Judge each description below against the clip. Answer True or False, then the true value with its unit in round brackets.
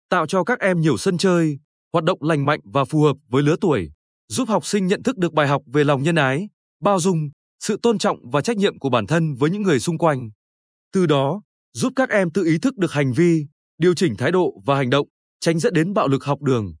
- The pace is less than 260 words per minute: True (250 wpm)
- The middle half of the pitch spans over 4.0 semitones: True (5.2 semitones)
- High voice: False (160 Hz)